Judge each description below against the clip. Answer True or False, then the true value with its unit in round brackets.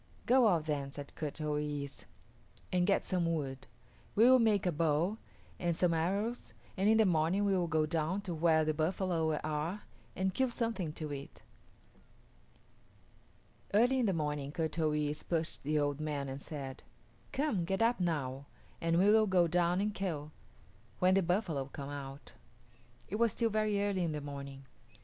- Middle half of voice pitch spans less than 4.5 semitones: False (4.8 semitones)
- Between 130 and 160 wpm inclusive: False (175 wpm)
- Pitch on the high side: False (165 Hz)